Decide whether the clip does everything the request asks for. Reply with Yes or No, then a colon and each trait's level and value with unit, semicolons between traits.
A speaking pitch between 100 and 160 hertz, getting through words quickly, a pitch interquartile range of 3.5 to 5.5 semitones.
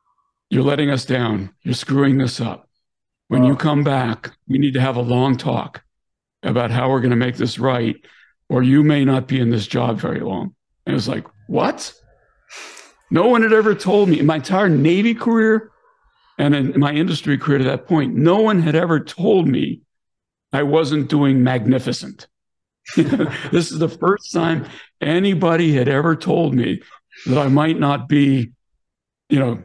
No: medium, 140 Hz; average, 180 wpm; average, 4.4 semitones